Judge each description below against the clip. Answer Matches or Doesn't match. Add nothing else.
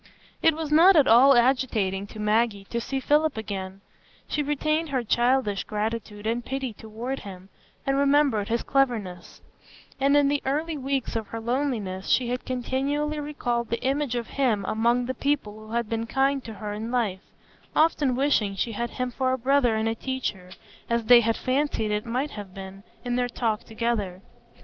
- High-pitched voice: Matches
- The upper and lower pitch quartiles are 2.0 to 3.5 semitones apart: Doesn't match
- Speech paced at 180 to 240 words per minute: Matches